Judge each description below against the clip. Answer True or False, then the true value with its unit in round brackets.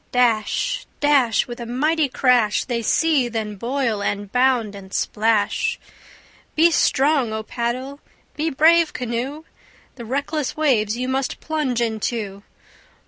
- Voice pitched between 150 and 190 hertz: False (250 Hz)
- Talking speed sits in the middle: False (130 wpm)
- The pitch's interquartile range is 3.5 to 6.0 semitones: True (4.6 semitones)